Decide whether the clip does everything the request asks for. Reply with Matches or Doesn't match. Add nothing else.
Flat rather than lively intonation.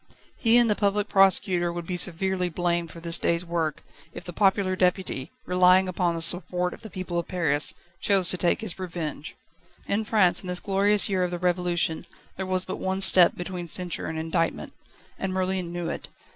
Matches